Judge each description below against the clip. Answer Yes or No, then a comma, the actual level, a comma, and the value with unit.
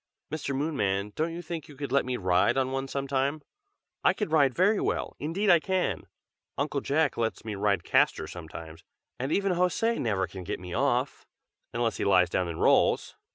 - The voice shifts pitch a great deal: Yes, wide, 8.1 semitones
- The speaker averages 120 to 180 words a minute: No, average, 195 wpm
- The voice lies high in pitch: No, low, 135 Hz